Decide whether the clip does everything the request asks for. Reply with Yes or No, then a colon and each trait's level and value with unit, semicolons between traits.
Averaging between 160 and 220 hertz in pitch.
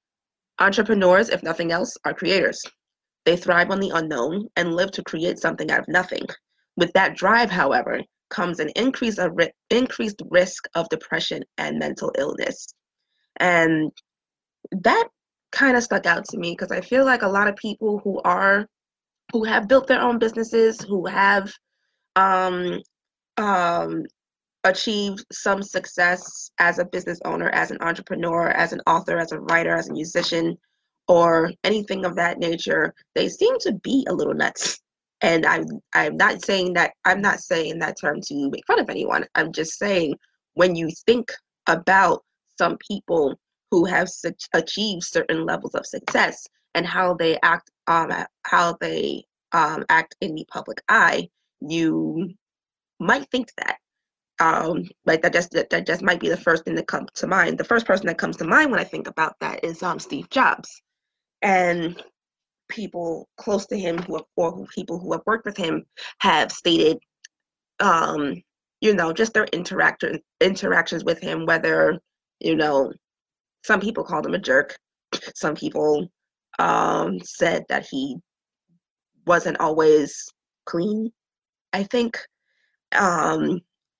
Yes: high, 190 Hz